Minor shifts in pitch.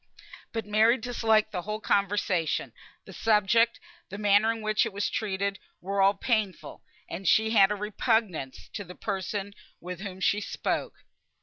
Yes: narrow, 2.1 semitones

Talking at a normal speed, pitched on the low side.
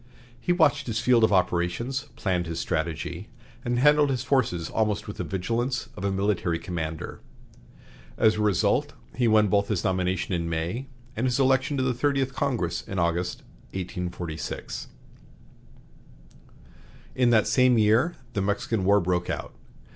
Yes: average, 150 wpm; low, 105 Hz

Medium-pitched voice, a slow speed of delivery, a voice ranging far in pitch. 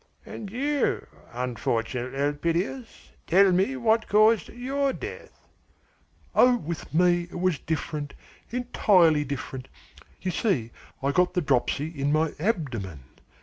Yes: medium, 170 Hz; slow, 120 wpm; wide, 7.3 semitones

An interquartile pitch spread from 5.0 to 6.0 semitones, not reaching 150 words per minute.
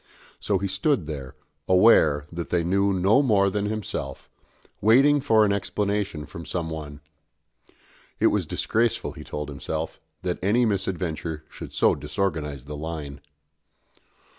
Yes: average, 5.3 semitones; average, 140 wpm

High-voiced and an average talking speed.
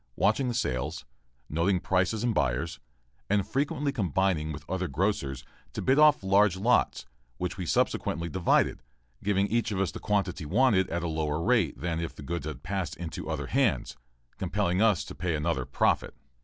No: very low, 90 Hz; average, 175 wpm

